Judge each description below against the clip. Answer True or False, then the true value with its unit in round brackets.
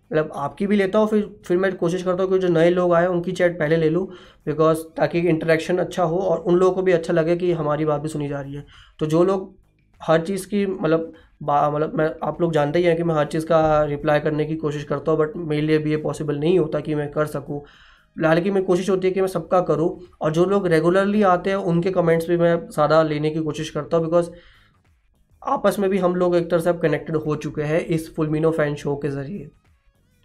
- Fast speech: True (240 wpm)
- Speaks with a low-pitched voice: False (165 Hz)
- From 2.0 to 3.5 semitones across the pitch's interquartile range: True (2.7 semitones)